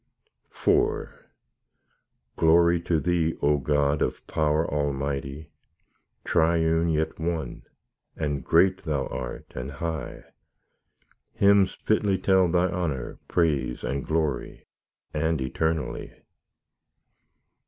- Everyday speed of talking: No, slow, 95 wpm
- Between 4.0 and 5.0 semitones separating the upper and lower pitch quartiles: No, average, 3.0 semitones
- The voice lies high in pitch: No, very low, 80 Hz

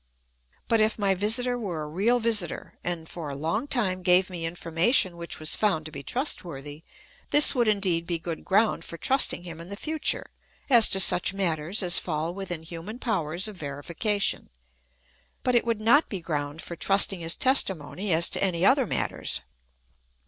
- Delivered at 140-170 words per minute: No, average, 180 wpm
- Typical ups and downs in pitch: Yes, average, 4.6 semitones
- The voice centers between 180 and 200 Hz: Yes, medium, 185 Hz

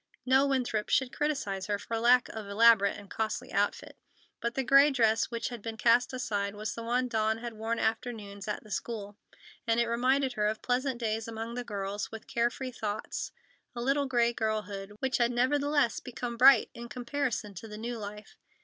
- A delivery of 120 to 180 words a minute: No, average, 190 wpm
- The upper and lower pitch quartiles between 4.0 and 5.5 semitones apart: No, average, 2.7 semitones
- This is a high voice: Yes, high, 230 Hz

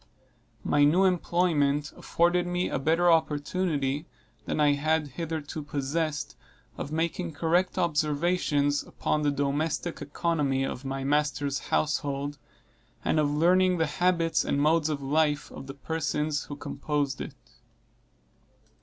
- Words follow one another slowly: Yes, slow, 125 wpm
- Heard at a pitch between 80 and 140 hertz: No, medium, 150 Hz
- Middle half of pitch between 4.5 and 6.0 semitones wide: No, narrow, 2.6 semitones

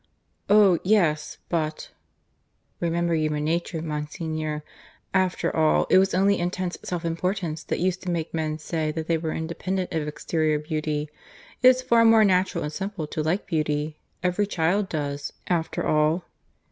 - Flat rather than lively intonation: No, average, 3.2 semitones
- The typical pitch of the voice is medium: Yes, medium, 165 Hz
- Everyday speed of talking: Yes, average, 155 wpm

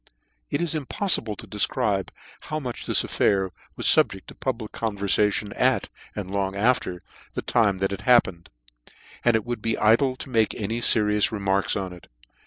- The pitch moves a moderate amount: Yes, average, 3.4 semitones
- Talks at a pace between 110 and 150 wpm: No, average, 180 wpm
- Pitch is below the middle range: Yes, low, 105 Hz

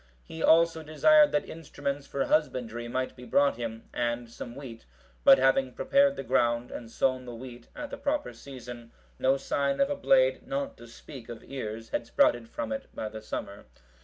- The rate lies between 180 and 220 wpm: Yes, average, 190 wpm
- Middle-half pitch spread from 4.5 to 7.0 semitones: Yes, average, 4.9 semitones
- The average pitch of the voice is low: Yes, low, 130 Hz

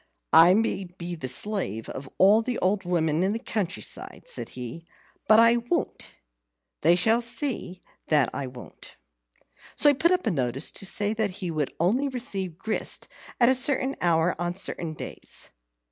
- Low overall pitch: No, high, 190 Hz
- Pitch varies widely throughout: Yes, wide, 5.8 semitones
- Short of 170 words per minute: No, average, 175 wpm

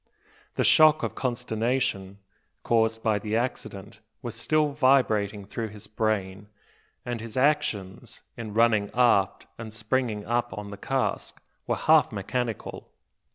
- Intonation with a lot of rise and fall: No, average, 3.1 semitones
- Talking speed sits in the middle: No, slow, 130 wpm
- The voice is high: No, low, 115 Hz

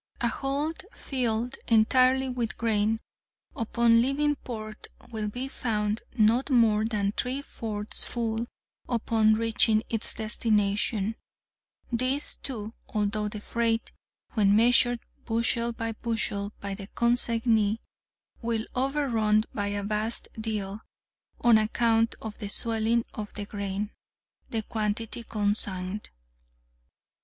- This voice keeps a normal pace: No, slow, 110 wpm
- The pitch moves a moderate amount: No, narrow, 1.9 semitones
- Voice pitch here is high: Yes, high, 225 Hz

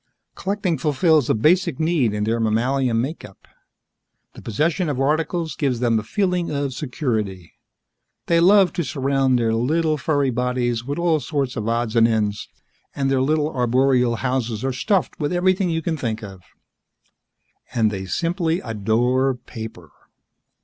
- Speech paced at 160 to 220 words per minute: No, average, 150 wpm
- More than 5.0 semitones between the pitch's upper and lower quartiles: Yes, wide, 5.6 semitones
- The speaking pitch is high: No, low, 130 Hz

